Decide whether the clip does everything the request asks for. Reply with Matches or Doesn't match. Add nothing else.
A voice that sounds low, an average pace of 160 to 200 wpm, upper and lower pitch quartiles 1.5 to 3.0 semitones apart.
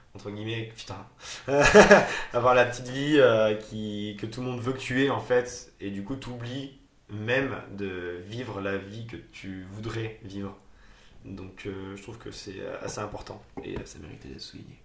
Doesn't match